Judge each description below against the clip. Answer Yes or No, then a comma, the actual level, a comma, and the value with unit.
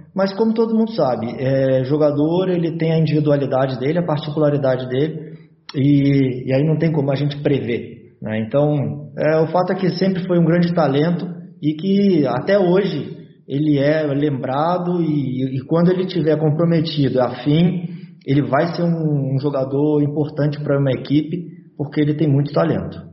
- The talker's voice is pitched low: No, medium, 150 Hz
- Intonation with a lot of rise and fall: No, average, 3.3 semitones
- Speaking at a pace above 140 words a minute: Yes, average, 170 wpm